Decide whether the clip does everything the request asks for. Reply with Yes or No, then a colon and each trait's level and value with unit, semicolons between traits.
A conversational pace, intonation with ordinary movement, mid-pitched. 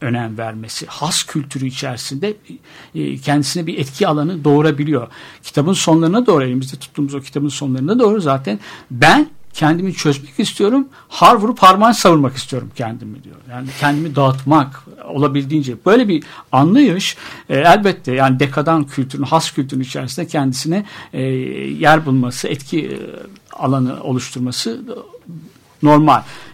Yes: average, 120 wpm; average, 3.8 semitones; medium, 145 Hz